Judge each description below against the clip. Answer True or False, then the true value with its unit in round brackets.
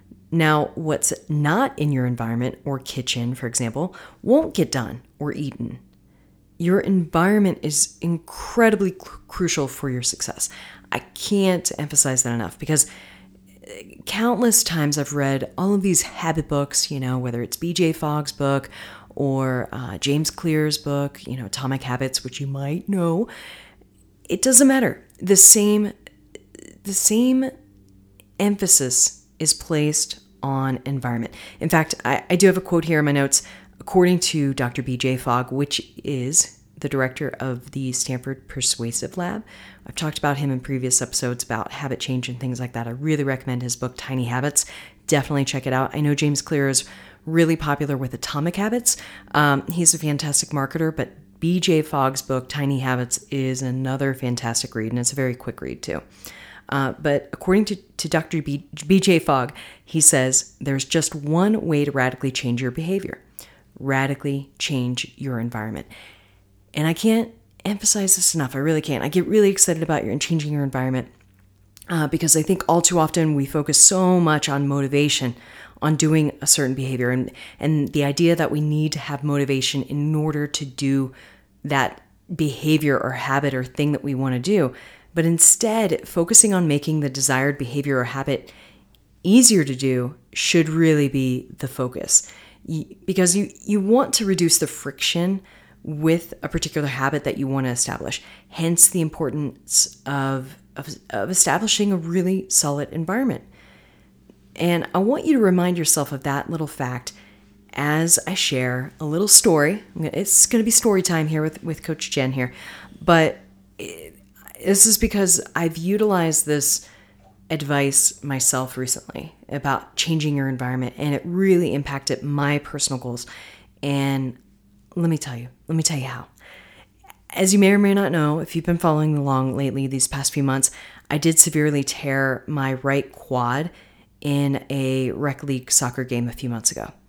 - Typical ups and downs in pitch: True (4.3 semitones)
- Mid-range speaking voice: True (145 Hz)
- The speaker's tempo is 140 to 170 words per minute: True (165 wpm)